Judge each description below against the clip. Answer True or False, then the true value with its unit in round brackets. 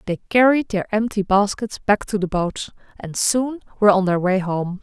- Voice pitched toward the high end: True (200 Hz)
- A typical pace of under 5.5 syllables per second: True (4.8 syllables/s)